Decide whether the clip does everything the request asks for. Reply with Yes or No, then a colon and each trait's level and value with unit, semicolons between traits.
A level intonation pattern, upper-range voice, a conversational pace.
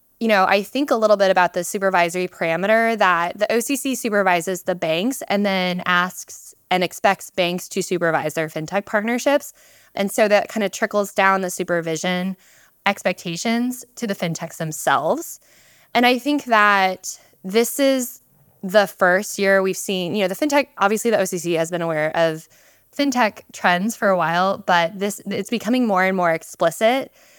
No: average, 4.0 semitones; high, 195 Hz; average, 170 wpm